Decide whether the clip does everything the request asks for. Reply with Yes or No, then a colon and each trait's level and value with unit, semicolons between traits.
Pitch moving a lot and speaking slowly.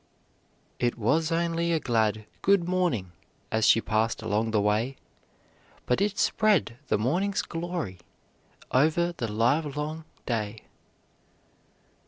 Yes: wide, 7.3 semitones; slow, 120 wpm